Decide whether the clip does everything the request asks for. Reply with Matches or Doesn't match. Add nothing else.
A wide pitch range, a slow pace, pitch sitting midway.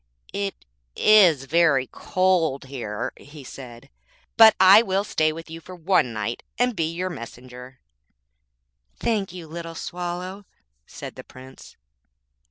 Matches